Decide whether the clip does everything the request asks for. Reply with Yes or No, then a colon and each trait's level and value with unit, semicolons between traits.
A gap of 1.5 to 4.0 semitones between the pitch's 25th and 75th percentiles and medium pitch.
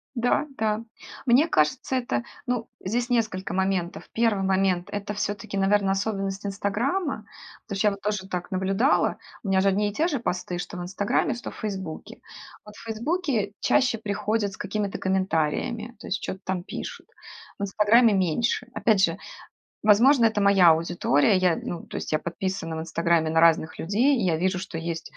No: average, 3.2 semitones; high, 200 Hz